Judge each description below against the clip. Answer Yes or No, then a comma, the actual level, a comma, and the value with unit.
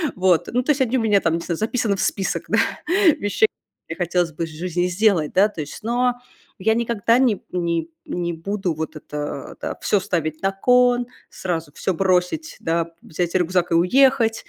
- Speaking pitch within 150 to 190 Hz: Yes, medium, 185 Hz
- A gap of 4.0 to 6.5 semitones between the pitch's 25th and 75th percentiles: Yes, average, 4.9 semitones